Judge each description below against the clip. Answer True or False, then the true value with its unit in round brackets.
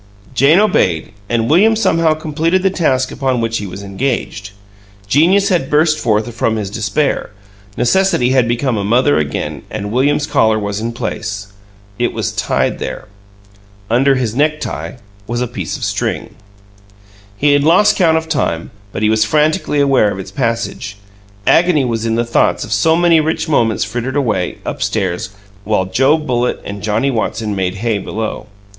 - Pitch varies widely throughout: True (6.0 semitones)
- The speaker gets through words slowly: False (170 wpm)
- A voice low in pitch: True (120 Hz)